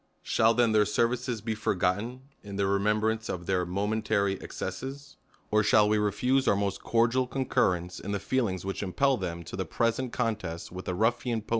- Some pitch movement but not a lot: Yes, average, 3.4 semitones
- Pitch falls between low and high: No, low, 105 Hz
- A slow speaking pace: No, average, 190 wpm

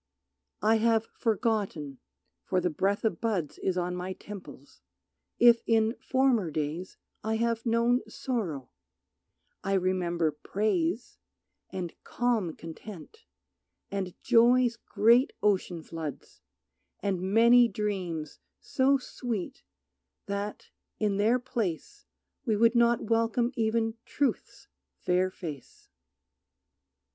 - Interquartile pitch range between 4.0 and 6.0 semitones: Yes, average, 4.5 semitones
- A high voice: Yes, high, 210 Hz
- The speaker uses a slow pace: Yes, slow, 105 wpm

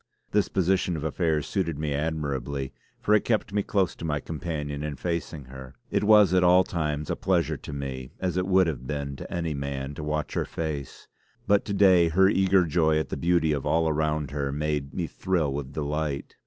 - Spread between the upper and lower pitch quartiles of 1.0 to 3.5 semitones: No, average, 3.9 semitones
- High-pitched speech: No, very low, 80 Hz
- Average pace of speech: No, fast, 210 wpm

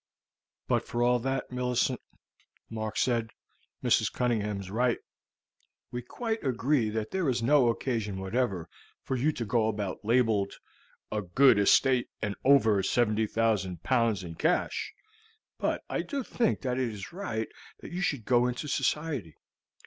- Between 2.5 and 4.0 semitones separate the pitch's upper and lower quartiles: Yes, average, 3.5 semitones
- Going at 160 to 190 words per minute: No, average, 150 wpm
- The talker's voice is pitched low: Yes, low, 120 Hz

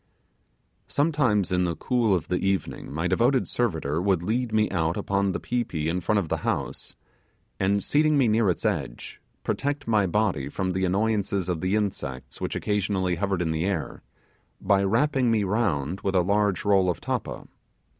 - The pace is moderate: Yes, average, 180 wpm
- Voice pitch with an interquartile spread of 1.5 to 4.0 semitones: Yes, average, 3.6 semitones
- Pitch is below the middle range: Yes, low, 100 Hz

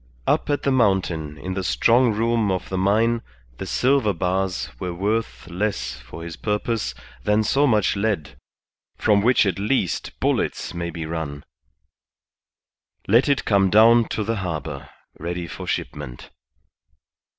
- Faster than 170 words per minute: No, average, 145 wpm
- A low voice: Yes, low, 100 Hz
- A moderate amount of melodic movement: Yes, average, 4.8 semitones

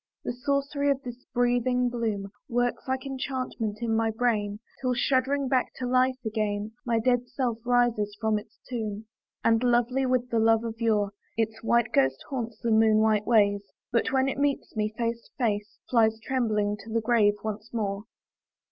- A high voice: Yes, high, 230 Hz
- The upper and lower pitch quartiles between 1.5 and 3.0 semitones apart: Yes, narrow, 2.5 semitones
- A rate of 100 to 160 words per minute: No, average, 175 wpm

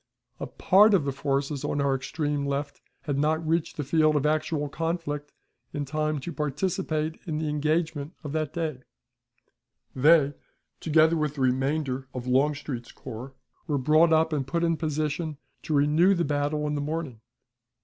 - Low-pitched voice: No, medium, 150 Hz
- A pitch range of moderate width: No, narrow, 2.0 semitones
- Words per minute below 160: No, average, 165 wpm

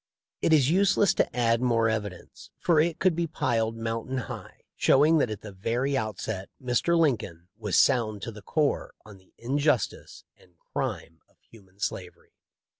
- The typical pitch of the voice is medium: No, low, 115 Hz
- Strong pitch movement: Yes, wide, 5.9 semitones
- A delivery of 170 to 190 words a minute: Yes, average, 175 wpm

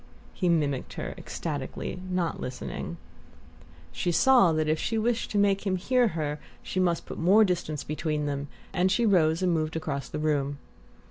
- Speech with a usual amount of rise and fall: Yes, average, 3.9 semitones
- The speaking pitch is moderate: Yes, medium, 170 Hz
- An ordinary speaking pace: Yes, average, 175 wpm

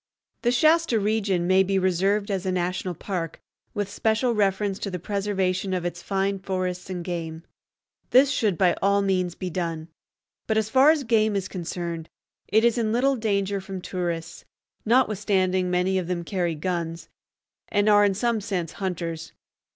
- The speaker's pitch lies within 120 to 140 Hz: No, high, 190 Hz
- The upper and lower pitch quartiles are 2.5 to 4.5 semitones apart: Yes, average, 2.8 semitones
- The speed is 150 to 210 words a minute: Yes, average, 165 wpm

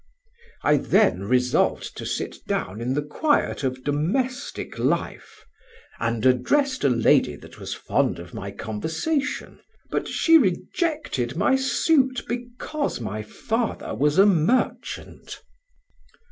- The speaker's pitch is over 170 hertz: No, medium, 155 Hz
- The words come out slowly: Yes, slow, 120 wpm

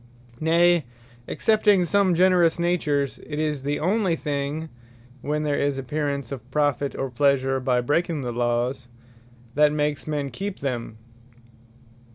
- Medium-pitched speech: Yes, medium, 145 Hz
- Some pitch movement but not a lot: Yes, average, 3.7 semitones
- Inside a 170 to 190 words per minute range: No, slow, 135 wpm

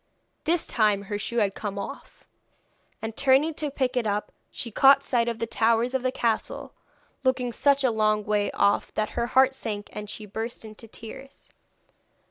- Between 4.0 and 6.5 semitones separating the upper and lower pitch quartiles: No, average, 3.6 semitones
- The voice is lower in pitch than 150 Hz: No, high, 230 Hz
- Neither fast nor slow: Yes, average, 180 wpm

